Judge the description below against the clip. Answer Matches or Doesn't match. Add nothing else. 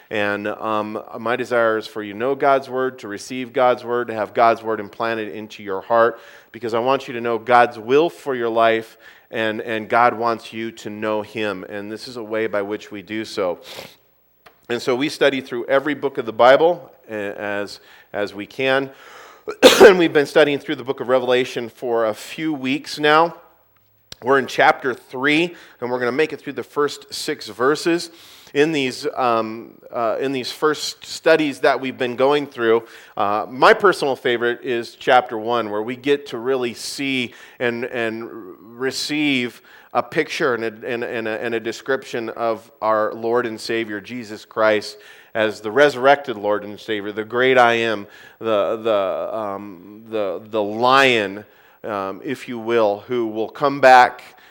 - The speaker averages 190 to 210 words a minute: Doesn't match